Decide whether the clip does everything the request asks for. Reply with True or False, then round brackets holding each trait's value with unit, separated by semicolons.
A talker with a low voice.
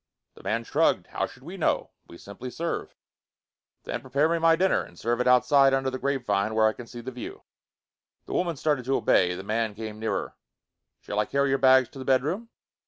True (125 Hz)